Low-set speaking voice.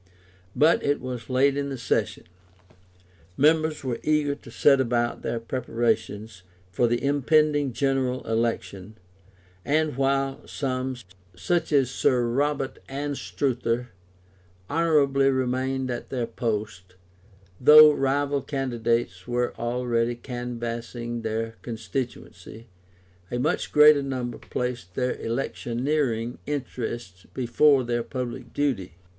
Yes: low, 125 Hz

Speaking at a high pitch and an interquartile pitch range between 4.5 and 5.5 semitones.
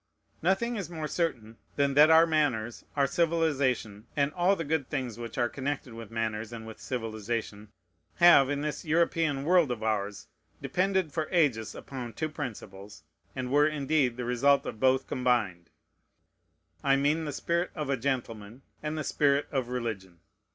No: low, 135 Hz; average, 5.2 semitones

